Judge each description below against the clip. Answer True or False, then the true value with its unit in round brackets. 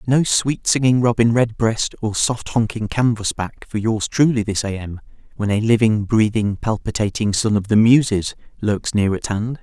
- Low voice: True (110 Hz)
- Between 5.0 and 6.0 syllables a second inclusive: False (4.6 syllables/s)